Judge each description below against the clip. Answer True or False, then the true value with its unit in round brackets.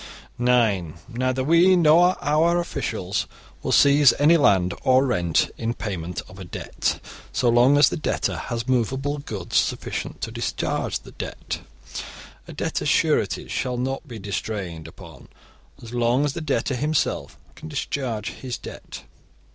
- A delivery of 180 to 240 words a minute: False (145 wpm)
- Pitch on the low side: True (125 Hz)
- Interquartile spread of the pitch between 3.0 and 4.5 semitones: False (5.5 semitones)